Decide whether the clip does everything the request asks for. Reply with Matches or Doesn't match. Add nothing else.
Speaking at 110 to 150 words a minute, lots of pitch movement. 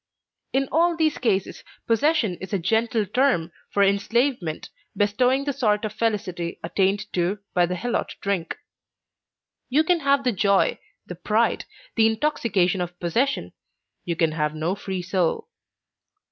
Matches